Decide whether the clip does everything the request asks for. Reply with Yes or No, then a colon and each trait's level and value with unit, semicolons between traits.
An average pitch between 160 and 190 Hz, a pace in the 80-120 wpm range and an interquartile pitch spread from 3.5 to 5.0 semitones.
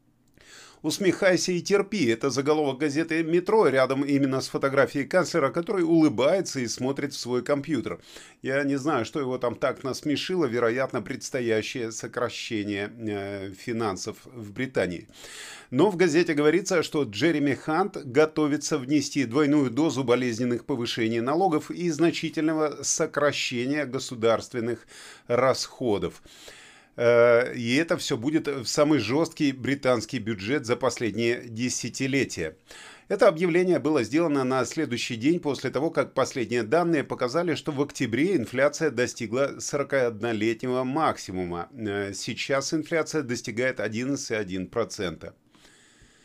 No: medium, 140 Hz; average, 115 wpm; average, 4.4 semitones